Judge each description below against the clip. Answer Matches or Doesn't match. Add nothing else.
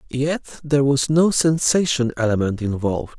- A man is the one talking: Matches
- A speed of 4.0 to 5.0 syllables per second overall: Matches